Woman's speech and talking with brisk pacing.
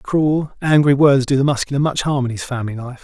No: male; fast, 235 wpm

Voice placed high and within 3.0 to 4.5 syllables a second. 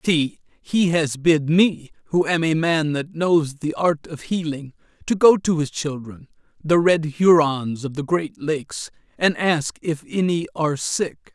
No: medium, 160 Hz; 4.0 syllables/s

